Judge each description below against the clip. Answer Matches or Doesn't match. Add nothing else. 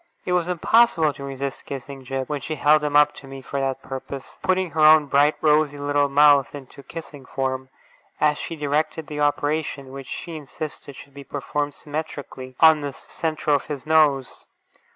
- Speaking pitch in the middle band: Matches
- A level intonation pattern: Matches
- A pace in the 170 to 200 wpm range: Matches